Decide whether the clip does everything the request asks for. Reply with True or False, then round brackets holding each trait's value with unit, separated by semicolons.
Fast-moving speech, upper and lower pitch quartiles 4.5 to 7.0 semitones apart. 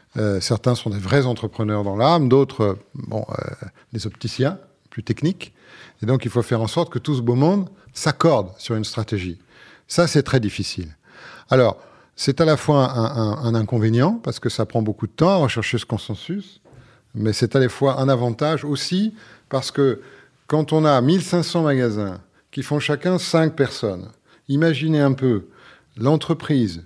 False (180 wpm; 5.1 semitones)